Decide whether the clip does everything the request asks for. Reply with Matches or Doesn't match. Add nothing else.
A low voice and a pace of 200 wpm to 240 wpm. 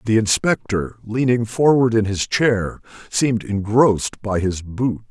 Doesn't match